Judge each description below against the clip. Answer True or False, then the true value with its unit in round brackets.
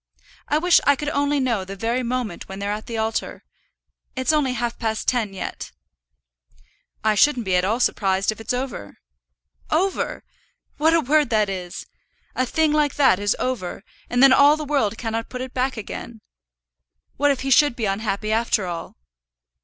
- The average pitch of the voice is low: False (240 Hz)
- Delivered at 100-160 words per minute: False (175 wpm)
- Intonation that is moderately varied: True (5.0 semitones)